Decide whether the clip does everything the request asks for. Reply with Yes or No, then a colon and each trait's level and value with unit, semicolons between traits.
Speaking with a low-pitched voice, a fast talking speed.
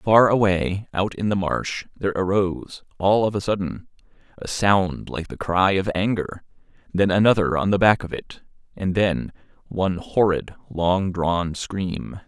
No: very low, 95 Hz; average, 160 wpm